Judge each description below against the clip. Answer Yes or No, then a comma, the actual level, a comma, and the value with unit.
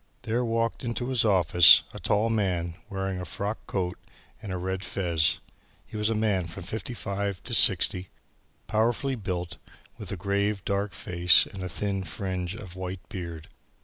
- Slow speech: No, average, 170 wpm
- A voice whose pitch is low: Yes, very low, 95 Hz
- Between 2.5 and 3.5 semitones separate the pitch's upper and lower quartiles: Yes, average, 3.0 semitones